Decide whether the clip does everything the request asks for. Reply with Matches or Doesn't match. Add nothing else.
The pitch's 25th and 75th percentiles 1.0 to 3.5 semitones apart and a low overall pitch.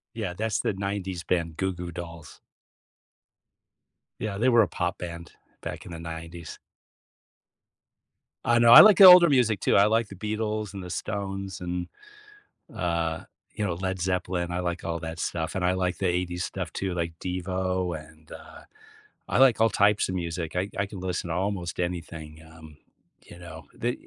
Matches